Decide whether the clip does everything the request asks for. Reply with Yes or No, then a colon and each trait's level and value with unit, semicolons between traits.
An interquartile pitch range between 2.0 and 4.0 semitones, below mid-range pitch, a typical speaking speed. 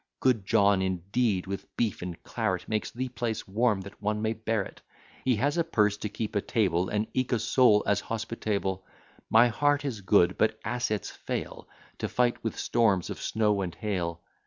Yes: average, 3.1 semitones; low, 105 Hz; average, 185 wpm